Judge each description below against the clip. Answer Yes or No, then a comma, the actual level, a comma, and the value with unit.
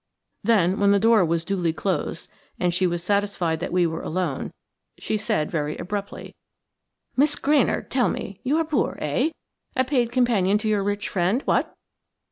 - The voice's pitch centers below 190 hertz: No, high, 200 Hz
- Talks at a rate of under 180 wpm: Yes, average, 165 wpm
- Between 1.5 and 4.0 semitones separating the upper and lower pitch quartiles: No, average, 5.2 semitones